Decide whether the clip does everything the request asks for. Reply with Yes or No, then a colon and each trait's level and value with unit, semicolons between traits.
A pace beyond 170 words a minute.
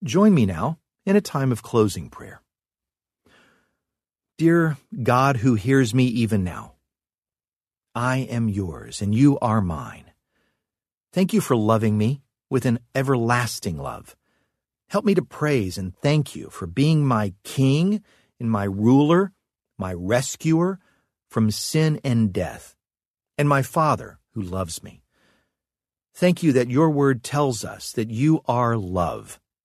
No: average, 140 wpm